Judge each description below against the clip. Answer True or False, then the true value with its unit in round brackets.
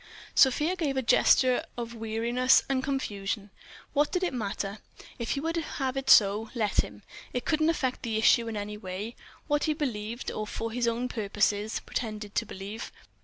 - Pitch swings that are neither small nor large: True (4.1 semitones)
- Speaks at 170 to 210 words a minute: True (175 wpm)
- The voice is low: False (230 Hz)